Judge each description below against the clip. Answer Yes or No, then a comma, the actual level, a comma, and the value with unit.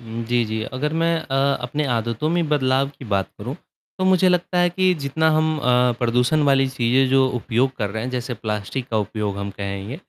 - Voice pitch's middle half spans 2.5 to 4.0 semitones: No, average, 4.7 semitones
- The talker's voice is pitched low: Yes, low, 130 Hz